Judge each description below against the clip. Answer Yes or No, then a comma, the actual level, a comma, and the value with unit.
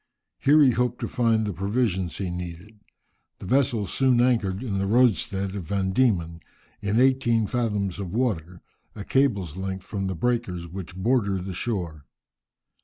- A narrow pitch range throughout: No, average, 4.4 semitones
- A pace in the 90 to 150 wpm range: No, average, 160 wpm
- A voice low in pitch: Yes, low, 100 Hz